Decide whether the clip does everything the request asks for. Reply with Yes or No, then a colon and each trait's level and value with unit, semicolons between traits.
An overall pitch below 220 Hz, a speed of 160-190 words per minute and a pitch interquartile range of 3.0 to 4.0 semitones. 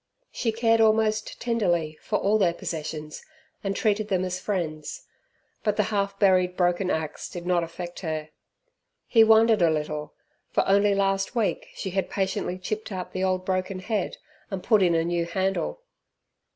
Yes: high, 190 Hz; average, 165 wpm; average, 3.4 semitones